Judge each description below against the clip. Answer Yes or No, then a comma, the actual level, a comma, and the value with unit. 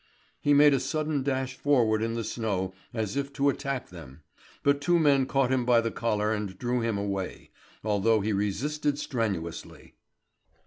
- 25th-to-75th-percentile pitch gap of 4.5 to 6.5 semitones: Yes, average, 5.0 semitones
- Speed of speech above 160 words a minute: Yes, average, 170 wpm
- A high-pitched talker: No, low, 120 Hz